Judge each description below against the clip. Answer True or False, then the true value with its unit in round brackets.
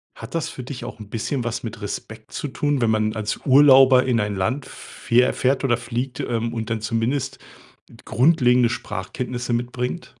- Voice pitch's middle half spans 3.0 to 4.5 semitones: False (2.6 semitones)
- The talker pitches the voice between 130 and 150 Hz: False (120 Hz)